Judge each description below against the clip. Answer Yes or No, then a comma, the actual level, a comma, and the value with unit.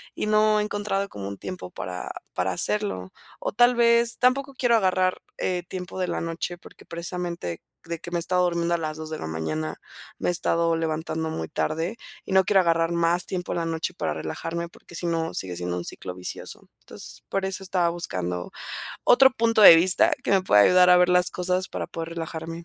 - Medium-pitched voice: Yes, medium, 170 Hz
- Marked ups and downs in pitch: No, average, 3.0 semitones